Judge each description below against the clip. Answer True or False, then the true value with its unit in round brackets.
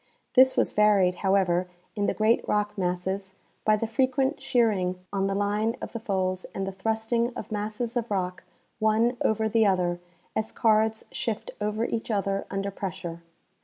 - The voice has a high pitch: True (210 Hz)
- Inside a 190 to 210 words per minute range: False (165 wpm)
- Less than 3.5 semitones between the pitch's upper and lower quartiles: True (2.6 semitones)